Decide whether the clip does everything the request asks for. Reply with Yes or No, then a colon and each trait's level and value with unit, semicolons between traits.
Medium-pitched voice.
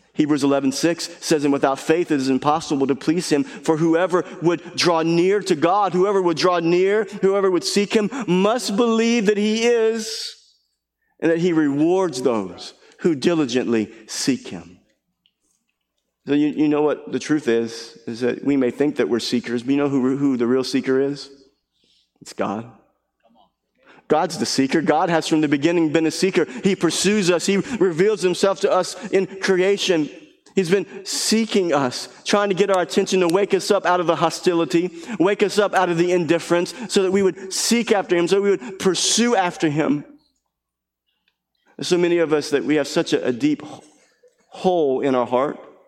Yes: medium, 170 Hz